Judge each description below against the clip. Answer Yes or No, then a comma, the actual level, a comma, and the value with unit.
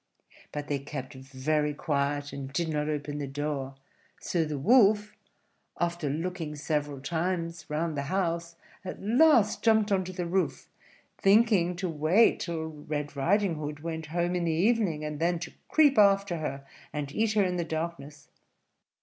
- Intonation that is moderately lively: Yes, average, 4.1 semitones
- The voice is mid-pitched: Yes, medium, 165 Hz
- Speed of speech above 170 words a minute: No, average, 165 wpm